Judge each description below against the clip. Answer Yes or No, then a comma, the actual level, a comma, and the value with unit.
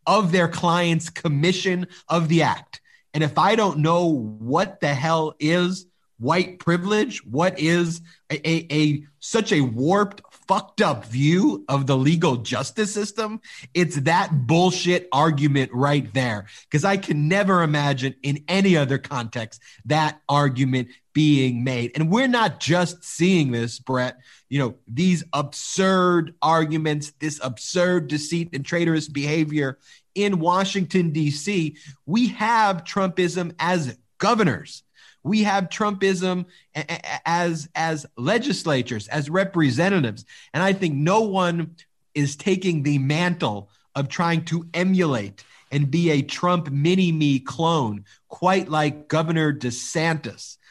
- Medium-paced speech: No, slow, 130 wpm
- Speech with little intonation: No, average, 4.1 semitones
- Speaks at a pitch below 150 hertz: No, medium, 160 Hz